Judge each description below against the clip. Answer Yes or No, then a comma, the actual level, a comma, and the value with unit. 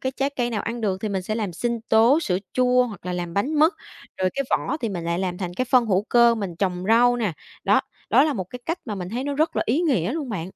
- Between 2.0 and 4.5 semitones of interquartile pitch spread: No, average, 5.3 semitones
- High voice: Yes, high, 225 Hz